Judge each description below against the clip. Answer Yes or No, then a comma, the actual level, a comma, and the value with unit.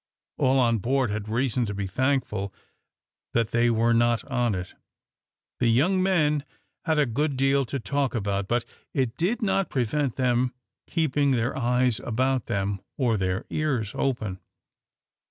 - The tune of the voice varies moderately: Yes, average, 3.6 semitones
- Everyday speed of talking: Yes, average, 155 wpm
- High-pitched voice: No, low, 125 Hz